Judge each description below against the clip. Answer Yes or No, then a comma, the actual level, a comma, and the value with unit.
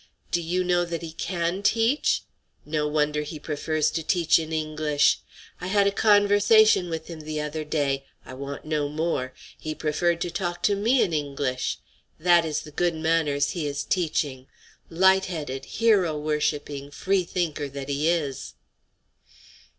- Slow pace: No, average, 160 wpm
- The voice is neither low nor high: Yes, medium, 160 Hz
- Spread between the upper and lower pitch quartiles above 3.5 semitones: No, average, 3.1 semitones